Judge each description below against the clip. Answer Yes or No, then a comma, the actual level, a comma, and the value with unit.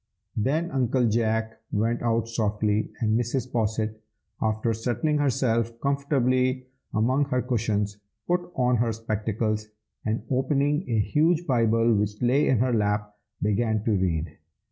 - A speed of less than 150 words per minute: Yes, slow, 135 wpm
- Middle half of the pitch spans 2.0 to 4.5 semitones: Yes, average, 3.0 semitones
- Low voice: Yes, low, 115 Hz